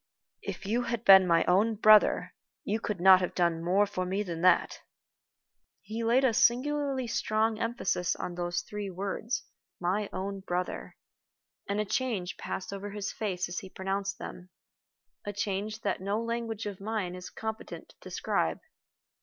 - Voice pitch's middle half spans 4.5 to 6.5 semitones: No, average, 3.2 semitones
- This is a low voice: No, high, 200 Hz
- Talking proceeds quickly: No, average, 160 wpm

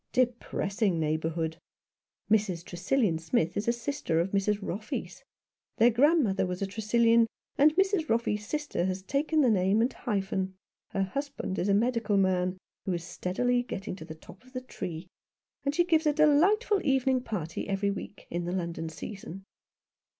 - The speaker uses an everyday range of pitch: No, wide, 5.7 semitones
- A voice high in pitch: Yes, high, 205 Hz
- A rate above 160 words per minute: Yes, average, 170 wpm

